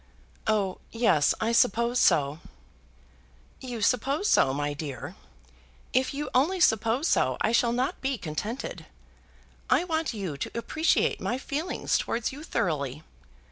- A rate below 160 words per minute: Yes, slow, 135 wpm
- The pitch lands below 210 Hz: No, high, 235 Hz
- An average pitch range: No, wide, 8.2 semitones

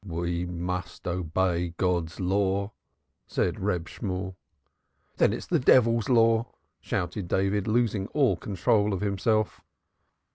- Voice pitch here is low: Yes, very low, 95 Hz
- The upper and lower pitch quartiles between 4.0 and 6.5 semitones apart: No, average, 3.4 semitones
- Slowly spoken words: Yes, slow, 120 wpm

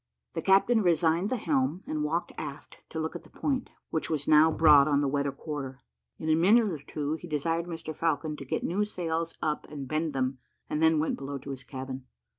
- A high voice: No, medium, 155 Hz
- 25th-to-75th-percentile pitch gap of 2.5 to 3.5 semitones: Yes, average, 2.8 semitones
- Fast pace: Yes, fast, 220 wpm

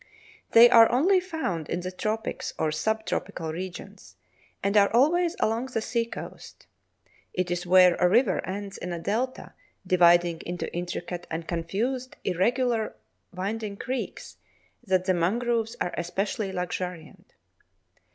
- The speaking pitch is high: Yes, high, 195 Hz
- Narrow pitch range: No, average, 4.8 semitones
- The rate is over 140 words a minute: No, slow, 135 wpm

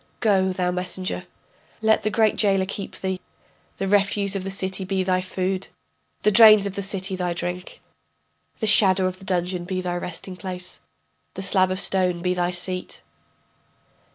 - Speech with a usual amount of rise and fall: No, narrow, 1.3 semitones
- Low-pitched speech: No, high, 190 Hz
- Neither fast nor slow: Yes, average, 170 wpm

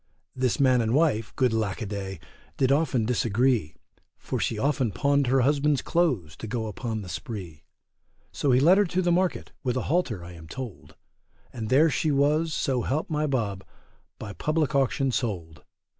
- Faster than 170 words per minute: Yes, average, 180 wpm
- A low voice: Yes, low, 125 Hz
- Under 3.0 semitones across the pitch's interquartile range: No, average, 5.2 semitones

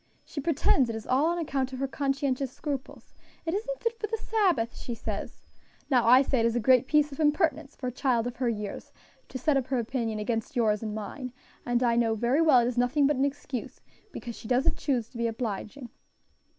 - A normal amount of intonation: Yes, average, 3.4 semitones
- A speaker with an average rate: No, fast, 220 wpm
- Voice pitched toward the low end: No, very high, 255 Hz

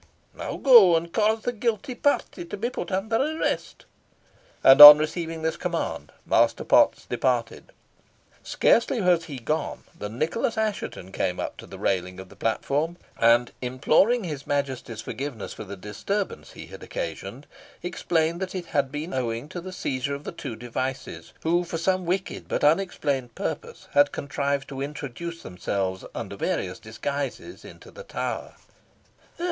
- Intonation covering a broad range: Yes, wide, 6.4 semitones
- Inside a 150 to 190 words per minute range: Yes, average, 155 wpm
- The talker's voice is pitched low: No, medium, 150 Hz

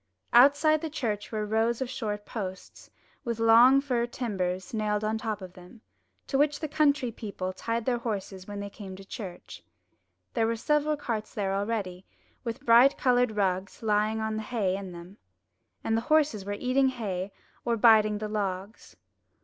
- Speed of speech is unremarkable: Yes, average, 180 wpm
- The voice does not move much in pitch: No, average, 3.4 semitones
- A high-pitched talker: Yes, high, 220 Hz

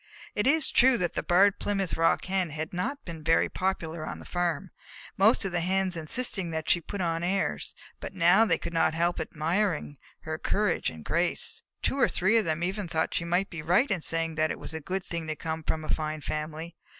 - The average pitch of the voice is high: No, medium, 175 Hz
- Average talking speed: No, fast, 220 wpm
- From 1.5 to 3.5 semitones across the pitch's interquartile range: Yes, average, 3.2 semitones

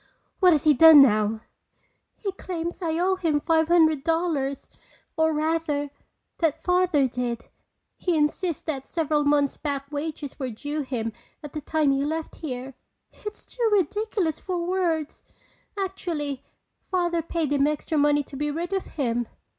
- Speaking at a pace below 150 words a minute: No, average, 155 wpm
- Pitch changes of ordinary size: Yes, average, 3.3 semitones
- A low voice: No, very high, 310 Hz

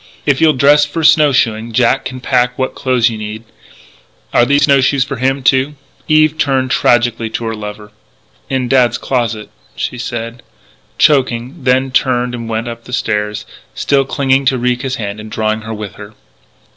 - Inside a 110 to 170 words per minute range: No, average, 180 wpm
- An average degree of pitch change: Yes, average, 3.0 semitones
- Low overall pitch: Yes, low, 125 Hz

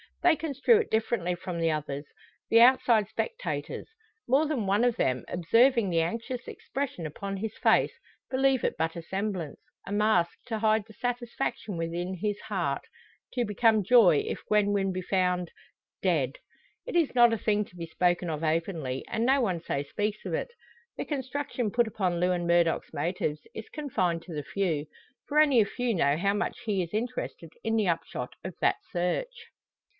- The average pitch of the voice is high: Yes, high, 200 Hz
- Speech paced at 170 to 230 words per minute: Yes, average, 180 wpm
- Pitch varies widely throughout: Yes, wide, 5.8 semitones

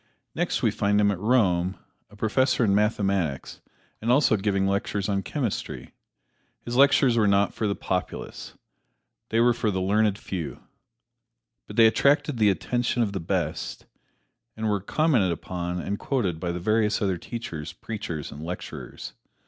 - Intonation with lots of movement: No, average, 3.6 semitones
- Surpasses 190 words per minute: No, average, 155 wpm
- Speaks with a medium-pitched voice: No, low, 100 Hz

